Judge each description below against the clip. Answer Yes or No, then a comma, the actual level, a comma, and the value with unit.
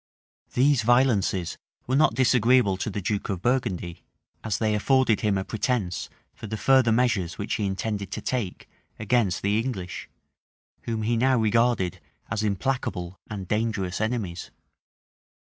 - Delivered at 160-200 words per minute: No, average, 145 wpm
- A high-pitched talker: No, low, 110 Hz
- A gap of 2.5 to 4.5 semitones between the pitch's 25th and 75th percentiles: Yes, average, 4.0 semitones